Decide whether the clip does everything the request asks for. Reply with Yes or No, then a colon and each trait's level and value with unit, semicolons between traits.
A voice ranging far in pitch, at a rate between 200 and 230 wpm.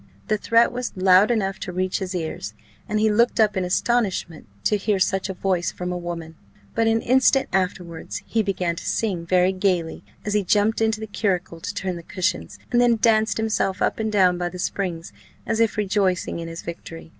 No: average, 3.5 semitones; fast, 205 wpm